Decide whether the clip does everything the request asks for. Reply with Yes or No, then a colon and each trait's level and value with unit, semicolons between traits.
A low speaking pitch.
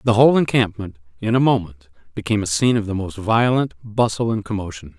Yes: low, 105 Hz